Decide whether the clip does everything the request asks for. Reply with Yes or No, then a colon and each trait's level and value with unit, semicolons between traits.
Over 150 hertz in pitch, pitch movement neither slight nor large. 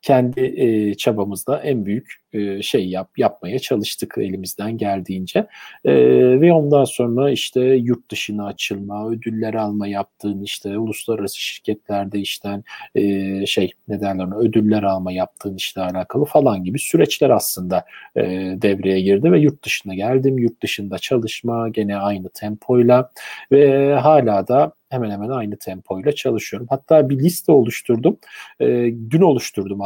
No: low, 105 Hz; average, 4.3 semitones